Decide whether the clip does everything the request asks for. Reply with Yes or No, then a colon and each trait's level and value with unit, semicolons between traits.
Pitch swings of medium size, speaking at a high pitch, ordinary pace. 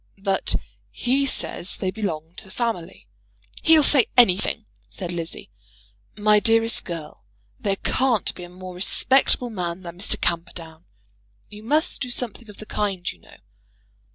Yes: average, 4.8 semitones; high, 200 Hz; average, 150 wpm